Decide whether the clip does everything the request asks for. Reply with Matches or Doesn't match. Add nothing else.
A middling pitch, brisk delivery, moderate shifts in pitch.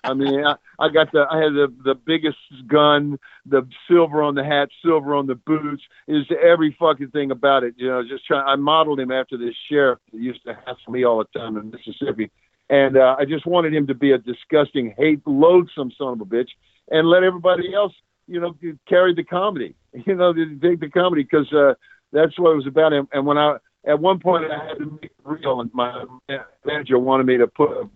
Matches